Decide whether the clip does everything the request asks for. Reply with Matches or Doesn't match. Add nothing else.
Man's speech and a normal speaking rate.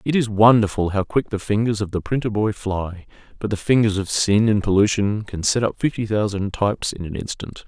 Doesn't match